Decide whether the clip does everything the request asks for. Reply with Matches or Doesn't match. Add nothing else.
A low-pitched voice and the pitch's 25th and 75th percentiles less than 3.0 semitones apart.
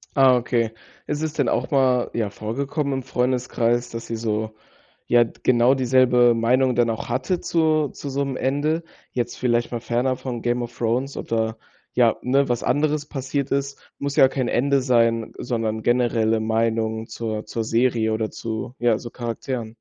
Matches